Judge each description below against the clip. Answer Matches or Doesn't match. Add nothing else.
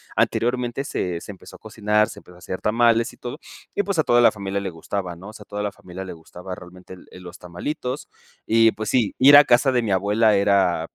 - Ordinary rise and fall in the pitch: Matches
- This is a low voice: Matches